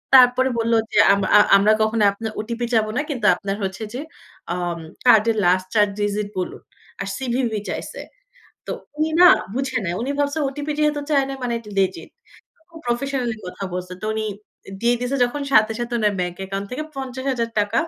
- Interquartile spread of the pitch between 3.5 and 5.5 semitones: Yes, average, 4.0 semitones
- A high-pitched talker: Yes, high, 230 Hz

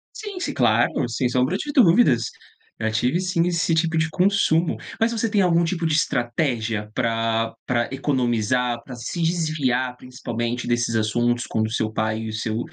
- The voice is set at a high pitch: No, low, 125 Hz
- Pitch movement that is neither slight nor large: No, wide, 6.4 semitones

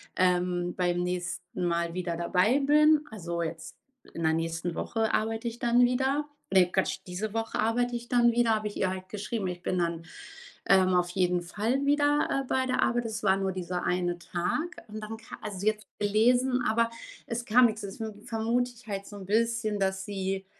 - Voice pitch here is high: Yes, high, 210 Hz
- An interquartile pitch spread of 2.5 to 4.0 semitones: No, average, 4.7 semitones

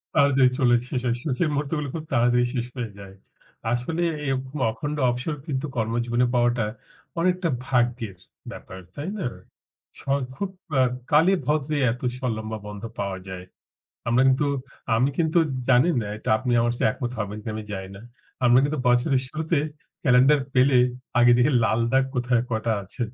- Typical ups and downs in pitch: Yes, average, 3.6 semitones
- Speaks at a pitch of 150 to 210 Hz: No, low, 125 Hz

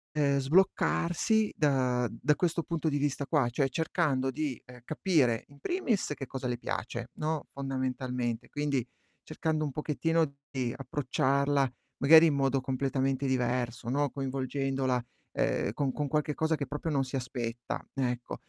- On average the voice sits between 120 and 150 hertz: Yes, medium, 140 Hz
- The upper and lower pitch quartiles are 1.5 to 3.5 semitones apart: Yes, average, 2.8 semitones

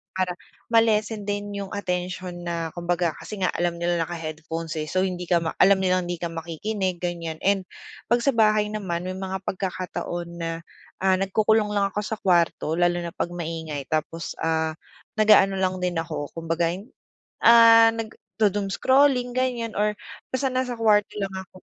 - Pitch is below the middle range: No, medium, 185 Hz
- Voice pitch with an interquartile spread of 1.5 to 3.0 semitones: No, average, 3.6 semitones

